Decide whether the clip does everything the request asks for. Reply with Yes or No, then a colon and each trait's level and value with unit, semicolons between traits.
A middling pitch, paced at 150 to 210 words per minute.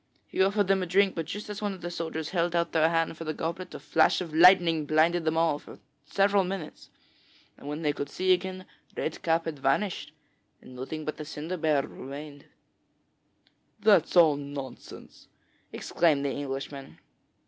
Yes: medium, 165 Hz; average, 180 wpm